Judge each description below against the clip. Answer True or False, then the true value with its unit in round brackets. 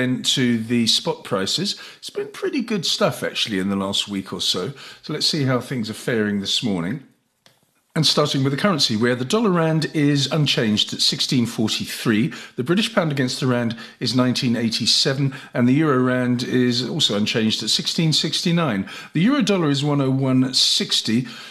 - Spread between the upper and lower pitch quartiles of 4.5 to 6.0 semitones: True (5.1 semitones)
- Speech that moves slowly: False (165 wpm)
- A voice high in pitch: False (130 Hz)